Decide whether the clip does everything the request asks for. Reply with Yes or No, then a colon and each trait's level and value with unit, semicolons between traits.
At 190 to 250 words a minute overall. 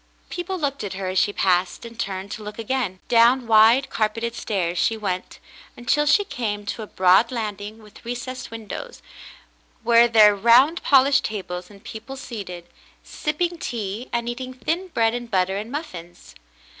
No: average, 165 wpm